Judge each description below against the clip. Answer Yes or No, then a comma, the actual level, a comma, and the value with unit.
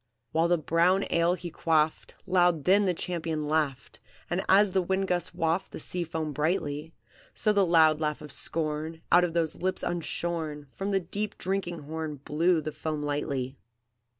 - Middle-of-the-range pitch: Yes, medium, 165 Hz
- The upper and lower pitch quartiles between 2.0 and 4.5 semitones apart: Yes, average, 2.8 semitones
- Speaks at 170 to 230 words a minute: Yes, average, 175 wpm